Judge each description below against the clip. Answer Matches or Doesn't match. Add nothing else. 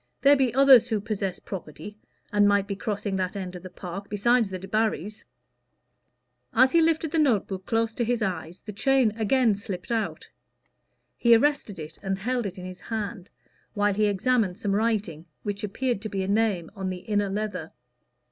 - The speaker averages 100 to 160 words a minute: Doesn't match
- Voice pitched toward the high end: Matches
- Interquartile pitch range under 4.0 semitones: Matches